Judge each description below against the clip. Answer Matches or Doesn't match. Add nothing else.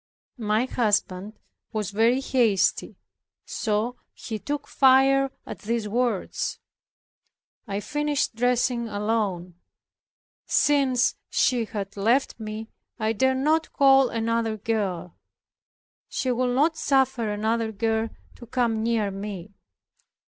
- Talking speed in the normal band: Doesn't match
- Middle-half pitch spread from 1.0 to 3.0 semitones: Doesn't match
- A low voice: Doesn't match